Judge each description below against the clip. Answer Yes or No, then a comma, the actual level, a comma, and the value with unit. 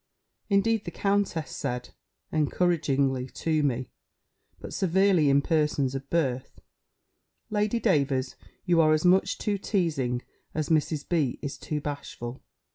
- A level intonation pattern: No, average, 4.8 semitones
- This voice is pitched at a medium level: Yes, medium, 155 Hz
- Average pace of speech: No, slow, 125 wpm